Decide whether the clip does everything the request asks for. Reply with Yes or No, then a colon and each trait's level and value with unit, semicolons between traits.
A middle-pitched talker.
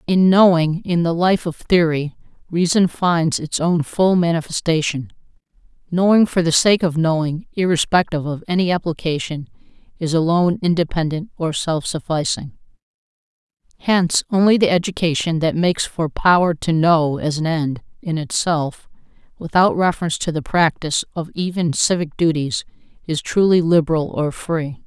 Yes: medium, 165 Hz